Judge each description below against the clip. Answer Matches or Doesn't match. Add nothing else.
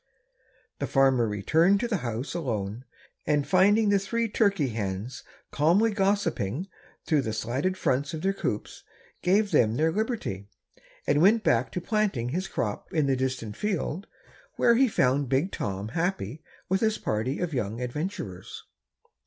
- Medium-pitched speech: Matches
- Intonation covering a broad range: Matches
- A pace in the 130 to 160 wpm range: Matches